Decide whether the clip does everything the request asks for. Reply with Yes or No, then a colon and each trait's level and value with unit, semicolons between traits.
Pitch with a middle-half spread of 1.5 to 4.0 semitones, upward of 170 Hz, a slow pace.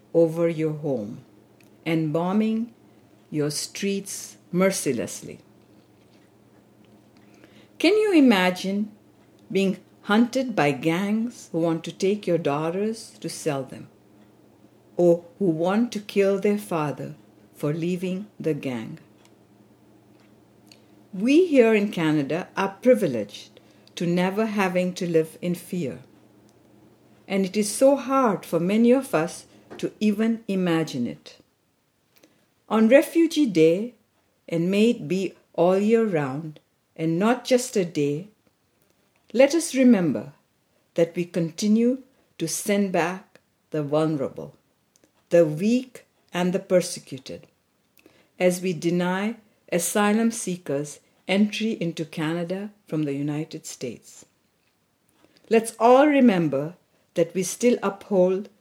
No: average, 5.2 semitones; medium, 185 Hz; slow, 115 wpm